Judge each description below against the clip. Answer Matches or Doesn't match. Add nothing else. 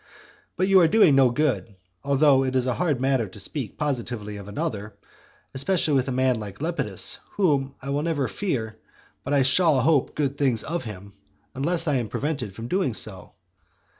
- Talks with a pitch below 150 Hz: Matches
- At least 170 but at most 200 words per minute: Matches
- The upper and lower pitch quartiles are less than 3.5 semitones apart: Doesn't match